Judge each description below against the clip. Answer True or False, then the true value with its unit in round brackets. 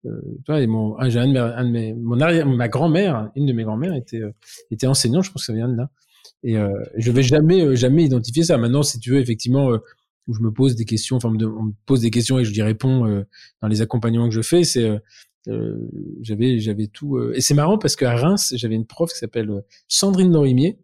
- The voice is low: True (125 Hz)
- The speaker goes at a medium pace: False (245 wpm)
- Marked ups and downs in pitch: False (4.1 semitones)